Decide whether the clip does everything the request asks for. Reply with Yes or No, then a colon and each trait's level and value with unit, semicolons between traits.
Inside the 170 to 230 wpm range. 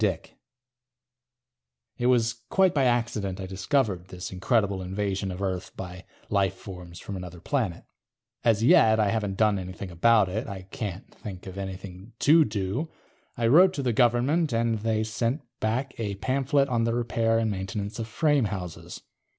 No: average, 160 wpm